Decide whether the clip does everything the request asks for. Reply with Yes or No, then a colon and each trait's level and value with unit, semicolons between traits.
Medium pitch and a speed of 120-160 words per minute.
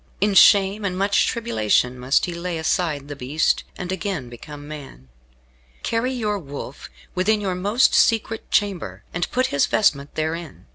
Yes: medium, 180 Hz; average, 155 wpm